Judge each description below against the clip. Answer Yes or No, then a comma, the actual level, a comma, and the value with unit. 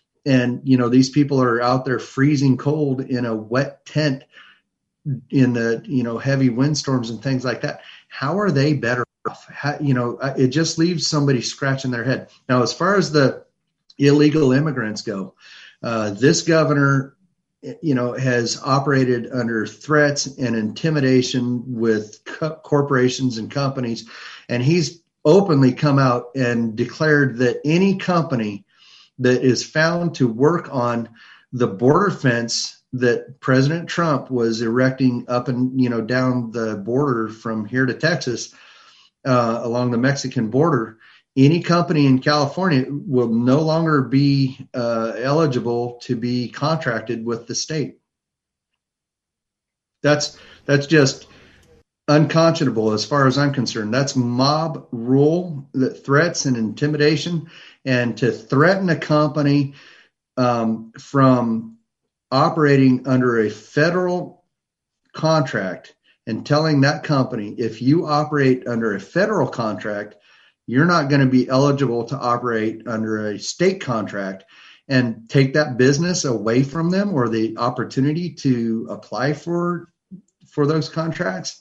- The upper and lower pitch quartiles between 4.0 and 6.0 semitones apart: No, average, 3.6 semitones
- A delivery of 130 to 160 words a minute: Yes, slow, 135 wpm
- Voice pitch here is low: Yes, low, 130 Hz